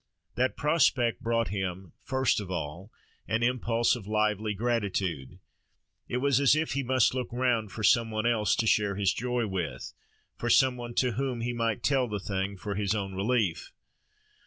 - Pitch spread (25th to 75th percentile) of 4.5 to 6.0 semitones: No, average, 3.7 semitones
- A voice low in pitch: Yes, low, 115 Hz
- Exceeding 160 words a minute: Yes, average, 180 wpm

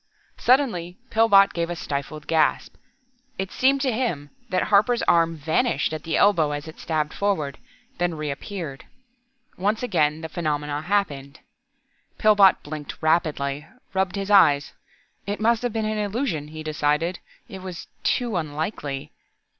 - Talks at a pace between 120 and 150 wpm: Yes, average, 140 wpm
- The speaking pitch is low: No, medium, 170 Hz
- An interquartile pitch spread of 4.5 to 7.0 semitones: Yes, average, 5.3 semitones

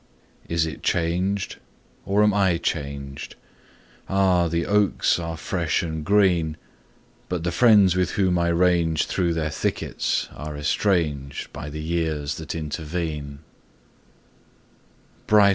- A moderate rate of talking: No, slow, 120 wpm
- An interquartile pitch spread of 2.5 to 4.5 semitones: Yes, average, 2.9 semitones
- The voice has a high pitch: No, very low, 85 Hz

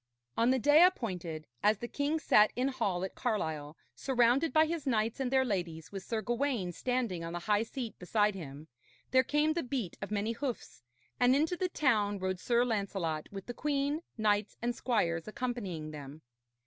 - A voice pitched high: Yes, high, 225 Hz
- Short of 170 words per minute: No, average, 185 wpm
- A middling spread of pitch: No, wide, 5.9 semitones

